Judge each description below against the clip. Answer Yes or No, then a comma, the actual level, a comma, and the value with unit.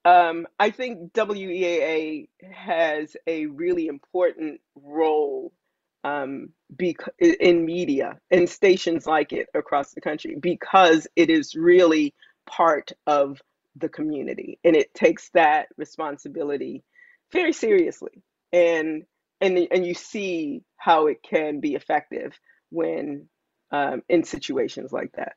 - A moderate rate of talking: No, slow, 120 wpm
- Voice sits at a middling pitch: Yes, medium, 180 Hz